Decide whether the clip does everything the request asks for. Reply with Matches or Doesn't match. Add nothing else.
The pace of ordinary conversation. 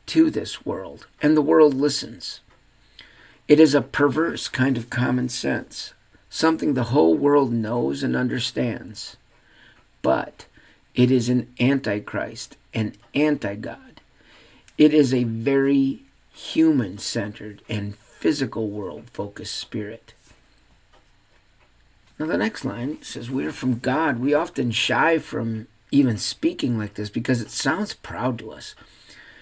Doesn't match